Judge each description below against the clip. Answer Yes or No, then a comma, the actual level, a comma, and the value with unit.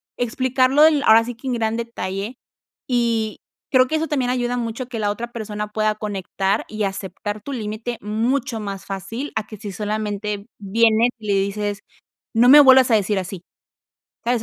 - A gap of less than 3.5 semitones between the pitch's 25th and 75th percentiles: Yes, average, 2.9 semitones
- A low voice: No, high, 220 Hz